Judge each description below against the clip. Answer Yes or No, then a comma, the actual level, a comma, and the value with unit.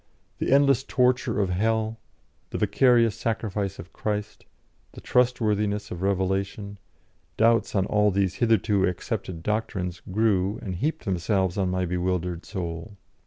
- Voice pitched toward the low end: Yes, low, 100 Hz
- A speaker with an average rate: No, slow, 130 wpm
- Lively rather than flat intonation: No, average, 3.3 semitones